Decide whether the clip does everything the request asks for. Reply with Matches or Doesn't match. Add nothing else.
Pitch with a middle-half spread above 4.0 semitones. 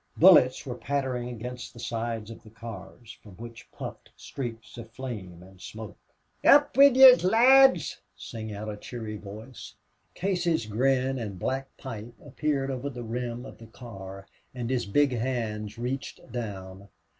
Doesn't match